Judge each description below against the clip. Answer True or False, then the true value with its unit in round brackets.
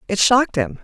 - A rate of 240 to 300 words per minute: False (215 wpm)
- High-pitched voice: True (225 Hz)